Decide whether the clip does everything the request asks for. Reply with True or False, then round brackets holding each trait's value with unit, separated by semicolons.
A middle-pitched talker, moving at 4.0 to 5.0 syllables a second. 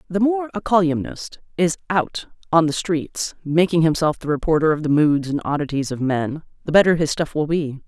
False (160 Hz; 5.2 syllables/s)